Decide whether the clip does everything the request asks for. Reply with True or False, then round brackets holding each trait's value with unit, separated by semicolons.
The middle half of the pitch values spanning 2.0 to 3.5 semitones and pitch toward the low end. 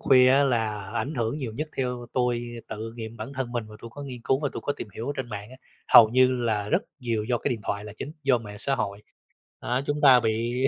True (3.2 semitones; 120 Hz)